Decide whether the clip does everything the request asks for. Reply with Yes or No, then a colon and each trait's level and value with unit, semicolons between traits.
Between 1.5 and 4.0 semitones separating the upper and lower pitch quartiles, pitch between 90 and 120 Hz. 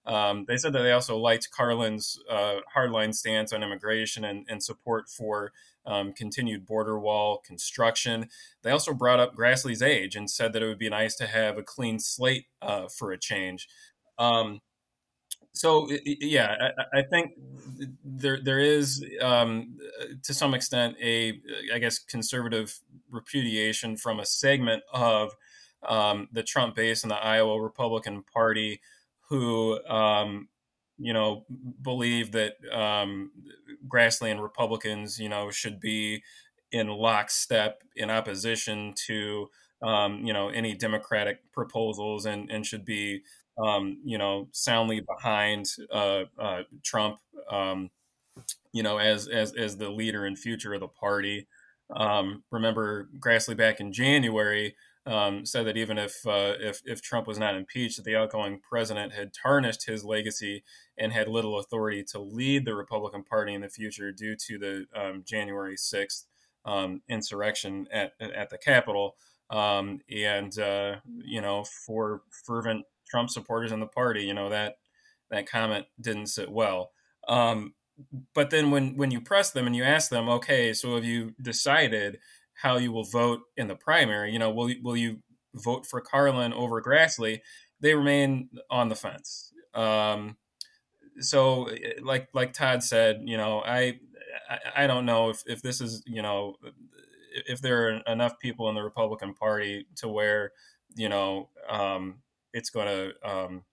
Yes: average, 2.8 semitones; low, 110 Hz